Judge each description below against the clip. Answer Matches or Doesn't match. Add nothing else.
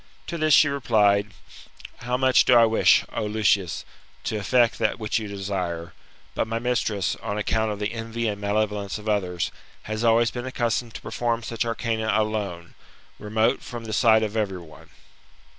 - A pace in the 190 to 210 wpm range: Doesn't match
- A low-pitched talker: Matches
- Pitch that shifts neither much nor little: Doesn't match